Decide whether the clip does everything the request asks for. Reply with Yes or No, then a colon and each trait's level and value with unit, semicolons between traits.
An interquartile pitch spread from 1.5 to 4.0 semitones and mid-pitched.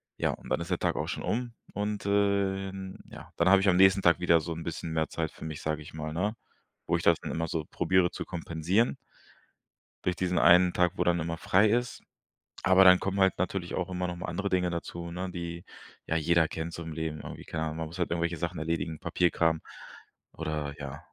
No: narrow, 2.4 semitones; very low, 85 Hz